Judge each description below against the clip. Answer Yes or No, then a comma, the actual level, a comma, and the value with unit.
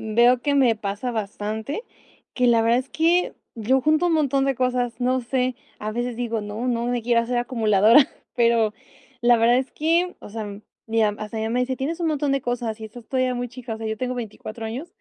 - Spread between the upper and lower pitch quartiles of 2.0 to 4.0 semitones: Yes, average, 2.7 semitones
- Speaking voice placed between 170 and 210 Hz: No, high, 245 Hz